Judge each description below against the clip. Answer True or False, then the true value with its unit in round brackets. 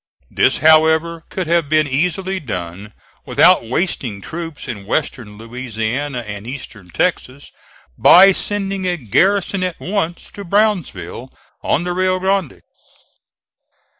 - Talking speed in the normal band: False (120 wpm)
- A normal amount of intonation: False (7.6 semitones)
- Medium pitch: True (160 Hz)